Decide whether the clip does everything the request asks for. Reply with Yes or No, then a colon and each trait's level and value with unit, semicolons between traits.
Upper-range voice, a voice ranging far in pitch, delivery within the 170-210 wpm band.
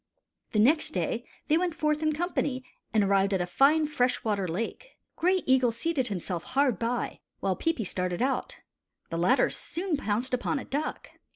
Yes: very high, 255 Hz; wide, 7.3 semitones; average, 175 wpm